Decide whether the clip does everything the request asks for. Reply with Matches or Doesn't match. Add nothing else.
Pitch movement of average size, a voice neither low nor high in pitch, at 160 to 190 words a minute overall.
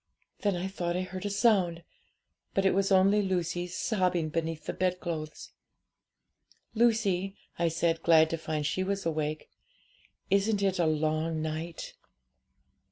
Doesn't match